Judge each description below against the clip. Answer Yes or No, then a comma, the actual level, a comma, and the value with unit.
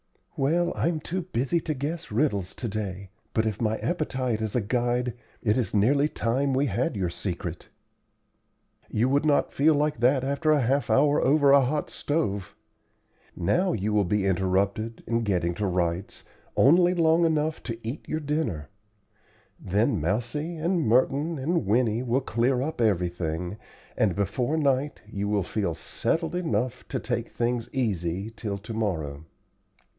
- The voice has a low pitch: Yes, low, 120 Hz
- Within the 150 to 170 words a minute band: Yes, average, 160 wpm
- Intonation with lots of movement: Yes, wide, 6.4 semitones